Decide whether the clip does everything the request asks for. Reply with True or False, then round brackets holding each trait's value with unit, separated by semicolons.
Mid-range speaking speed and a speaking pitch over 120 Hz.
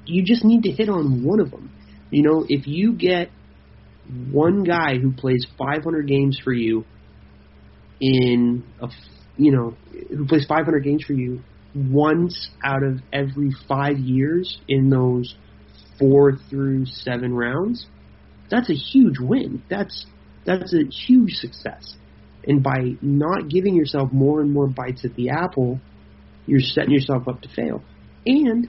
True (150 wpm; 135 Hz)